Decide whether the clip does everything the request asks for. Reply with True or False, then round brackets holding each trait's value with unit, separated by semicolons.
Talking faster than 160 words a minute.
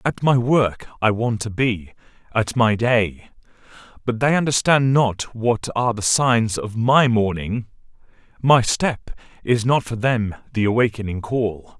False (145 wpm)